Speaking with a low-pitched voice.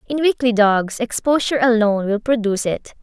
No: high, 230 Hz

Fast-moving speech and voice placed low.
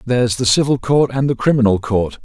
Yes: fast, 240 wpm; low, 125 Hz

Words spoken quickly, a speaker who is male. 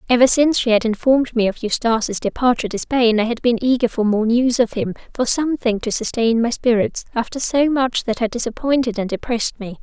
No: fast, 215 wpm; female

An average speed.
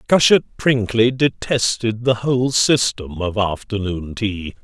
No: slow, 115 wpm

